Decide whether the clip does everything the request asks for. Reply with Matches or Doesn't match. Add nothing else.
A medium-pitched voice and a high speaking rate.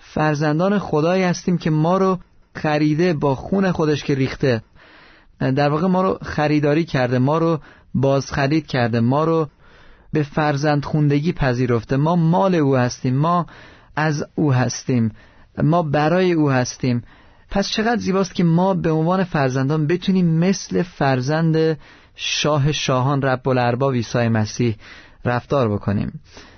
Doesn't match